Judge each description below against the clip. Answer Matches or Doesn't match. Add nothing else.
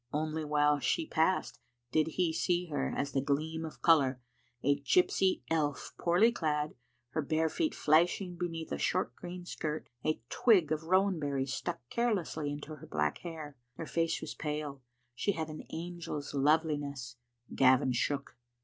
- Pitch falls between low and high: Matches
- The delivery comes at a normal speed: Matches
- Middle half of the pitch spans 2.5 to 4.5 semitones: Matches